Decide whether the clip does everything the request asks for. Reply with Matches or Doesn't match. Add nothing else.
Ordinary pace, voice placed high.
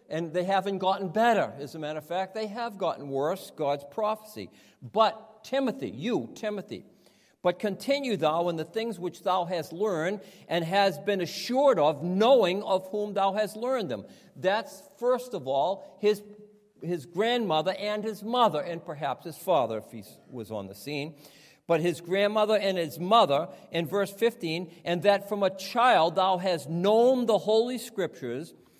Matches